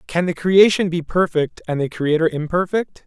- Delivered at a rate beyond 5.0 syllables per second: No, 4.9 syllables/s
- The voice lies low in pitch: No, medium, 170 Hz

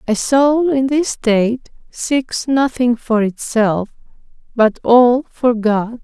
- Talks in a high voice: Yes, high, 245 Hz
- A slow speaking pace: Yes, slow, 130 wpm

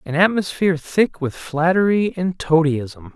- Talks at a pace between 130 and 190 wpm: Yes, slow, 135 wpm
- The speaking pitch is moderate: Yes, medium, 165 Hz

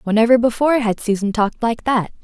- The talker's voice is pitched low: No, high, 230 Hz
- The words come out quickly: No, average, 190 wpm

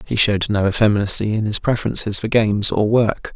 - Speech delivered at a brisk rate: No, average, 195 wpm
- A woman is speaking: No, male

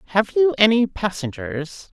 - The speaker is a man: No, female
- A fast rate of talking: No, slow, 120 wpm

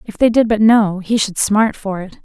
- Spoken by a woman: Yes, female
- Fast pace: Yes, fast, 270 wpm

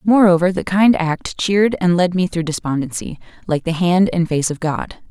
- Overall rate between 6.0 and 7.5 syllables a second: No, 4.9 syllables/s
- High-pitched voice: No, medium, 175 Hz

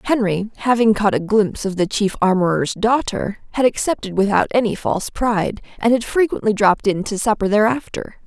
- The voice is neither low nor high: No, high, 210 Hz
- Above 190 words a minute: No, average, 175 wpm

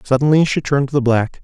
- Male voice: Yes, male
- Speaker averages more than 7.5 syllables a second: No, 6.8 syllables/s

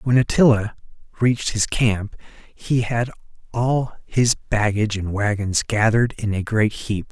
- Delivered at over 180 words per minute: No, average, 145 wpm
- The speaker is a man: Yes, male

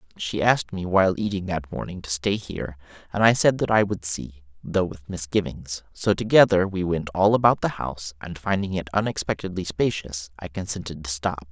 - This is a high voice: No, very low, 90 Hz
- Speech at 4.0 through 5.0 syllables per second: No, 5.4 syllables/s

